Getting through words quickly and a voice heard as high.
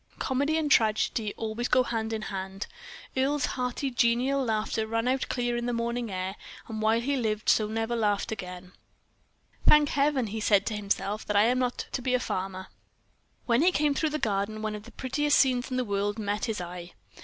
Yes: fast, 210 wpm; high, 225 Hz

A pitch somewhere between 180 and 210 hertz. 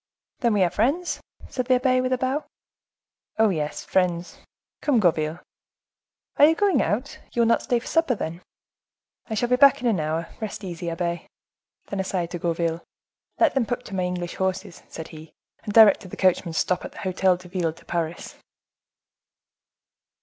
Yes: high, 190 Hz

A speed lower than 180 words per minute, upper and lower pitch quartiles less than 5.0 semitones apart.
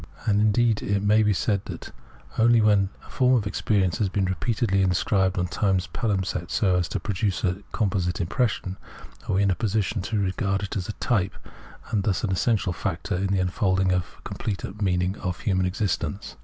No: average, 195 wpm; narrow, 2.4 semitones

